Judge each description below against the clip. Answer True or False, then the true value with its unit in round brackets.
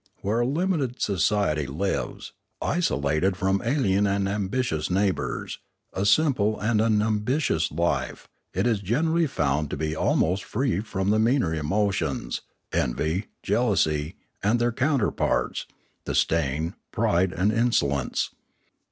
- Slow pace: True (120 wpm)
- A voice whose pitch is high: False (100 Hz)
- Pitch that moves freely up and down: True (6.4 semitones)